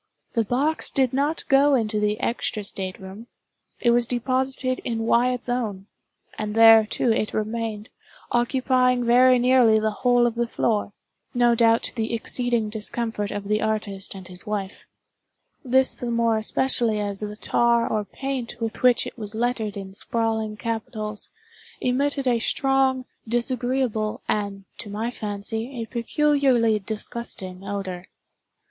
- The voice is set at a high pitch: Yes, high, 230 Hz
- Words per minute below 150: Yes, average, 140 wpm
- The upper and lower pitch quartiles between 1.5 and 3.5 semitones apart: Yes, average, 2.8 semitones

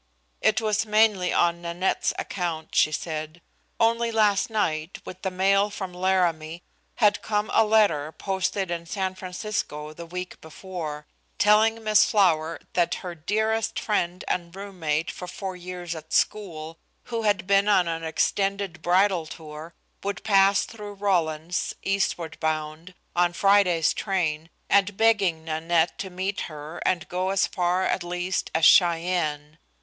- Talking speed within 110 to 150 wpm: Yes, average, 145 wpm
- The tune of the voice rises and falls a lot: No, average, 3.5 semitones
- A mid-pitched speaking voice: Yes, medium, 180 Hz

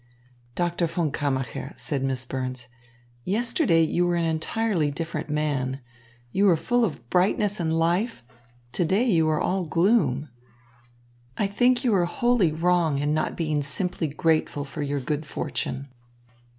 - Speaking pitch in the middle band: Yes, medium, 165 Hz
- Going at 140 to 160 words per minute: Yes, average, 150 wpm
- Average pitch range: Yes, average, 4.5 semitones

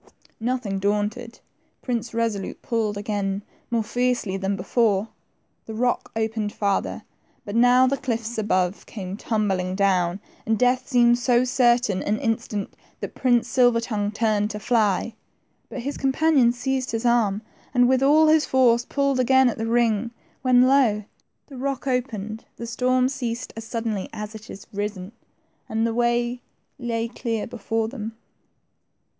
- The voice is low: No, high, 230 Hz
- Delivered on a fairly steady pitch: No, average, 3.0 semitones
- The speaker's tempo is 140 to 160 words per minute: Yes, average, 150 wpm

